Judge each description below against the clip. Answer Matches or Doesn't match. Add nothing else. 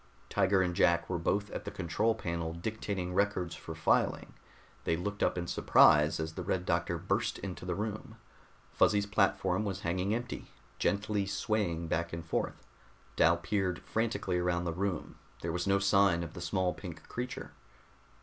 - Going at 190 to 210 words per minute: Doesn't match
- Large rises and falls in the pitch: Doesn't match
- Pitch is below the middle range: Matches